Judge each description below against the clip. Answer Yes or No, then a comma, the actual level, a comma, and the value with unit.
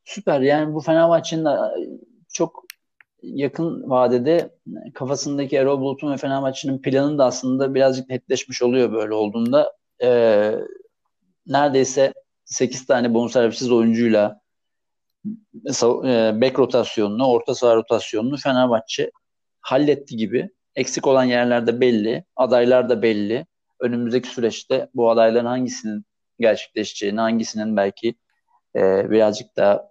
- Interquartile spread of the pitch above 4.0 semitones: No, average, 3.7 semitones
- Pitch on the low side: Yes, low, 130 Hz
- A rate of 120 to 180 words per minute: No, average, 110 wpm